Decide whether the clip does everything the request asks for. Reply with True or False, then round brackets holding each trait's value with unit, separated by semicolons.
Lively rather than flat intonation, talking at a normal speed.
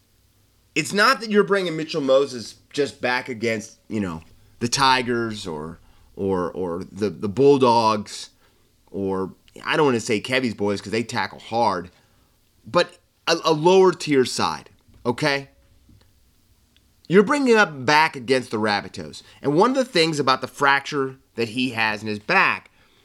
True (5.9 semitones; 155 wpm)